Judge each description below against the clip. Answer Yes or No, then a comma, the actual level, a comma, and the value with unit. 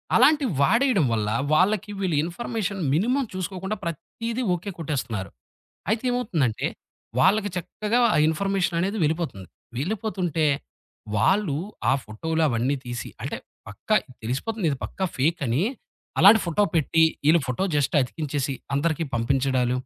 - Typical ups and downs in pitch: No, wide, 6.9 semitones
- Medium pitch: Yes, medium, 170 Hz